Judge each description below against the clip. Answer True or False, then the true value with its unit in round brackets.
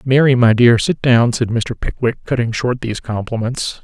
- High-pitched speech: False (120 Hz)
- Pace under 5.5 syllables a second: True (4.8 syllables/s)